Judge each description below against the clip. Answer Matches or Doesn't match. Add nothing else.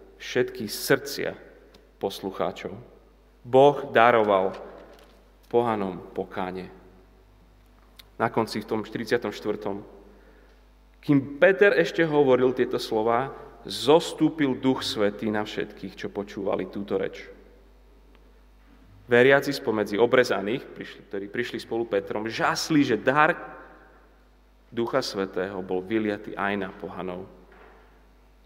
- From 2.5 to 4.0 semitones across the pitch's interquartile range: Doesn't match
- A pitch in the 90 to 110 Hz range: Matches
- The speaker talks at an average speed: Doesn't match